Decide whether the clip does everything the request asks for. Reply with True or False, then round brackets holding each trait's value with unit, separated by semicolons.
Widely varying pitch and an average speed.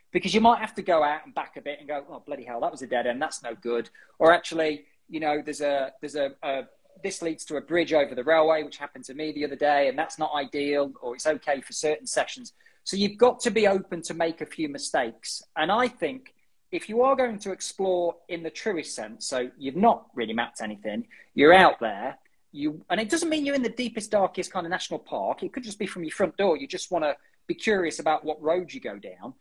False (7.0 semitones; 255 wpm)